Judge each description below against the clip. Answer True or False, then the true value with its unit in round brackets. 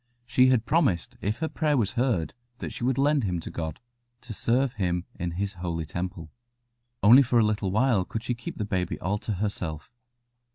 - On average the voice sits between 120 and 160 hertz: False (105 Hz)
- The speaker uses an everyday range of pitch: False (5.7 semitones)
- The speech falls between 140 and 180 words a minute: False (200 wpm)